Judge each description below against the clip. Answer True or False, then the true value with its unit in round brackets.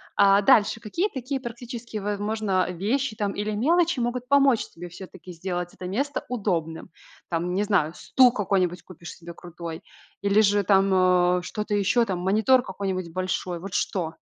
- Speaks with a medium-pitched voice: False (200 Hz)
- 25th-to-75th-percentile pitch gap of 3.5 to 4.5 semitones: True (4.2 semitones)